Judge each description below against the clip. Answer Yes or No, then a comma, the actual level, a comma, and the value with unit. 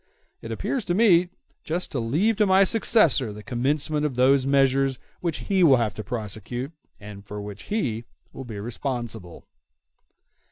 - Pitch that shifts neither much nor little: No, wide, 7.1 semitones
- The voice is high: No, low, 130 Hz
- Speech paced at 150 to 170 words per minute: Yes, average, 160 wpm